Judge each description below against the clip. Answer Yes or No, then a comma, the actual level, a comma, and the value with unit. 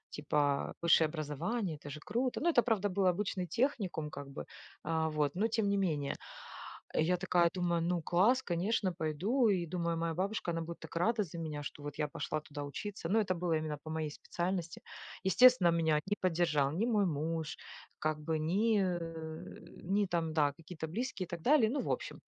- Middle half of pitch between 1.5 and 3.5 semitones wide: No, average, 4.1 semitones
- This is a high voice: No, medium, 170 Hz